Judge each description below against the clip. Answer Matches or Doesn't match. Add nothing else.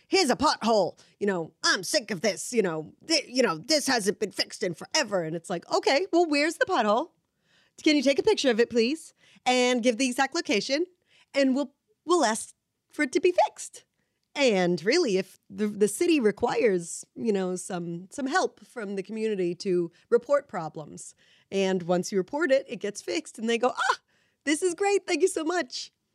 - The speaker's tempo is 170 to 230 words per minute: Matches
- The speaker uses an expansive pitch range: Matches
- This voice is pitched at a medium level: Doesn't match